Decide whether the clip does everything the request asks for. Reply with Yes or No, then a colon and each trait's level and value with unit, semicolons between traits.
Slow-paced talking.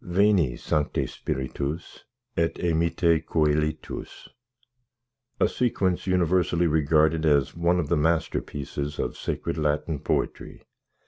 Yes: slow, 105 wpm